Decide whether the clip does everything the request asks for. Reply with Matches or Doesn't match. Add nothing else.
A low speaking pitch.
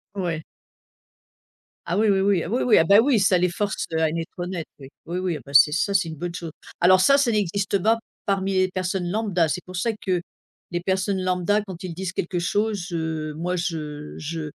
Doesn't match